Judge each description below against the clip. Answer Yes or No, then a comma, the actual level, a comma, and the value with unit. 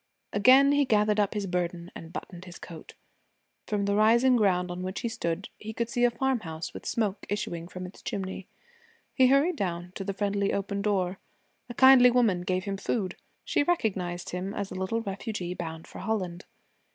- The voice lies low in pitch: No, high, 200 Hz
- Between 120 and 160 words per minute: No, average, 190 wpm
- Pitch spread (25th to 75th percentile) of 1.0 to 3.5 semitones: No, average, 3.9 semitones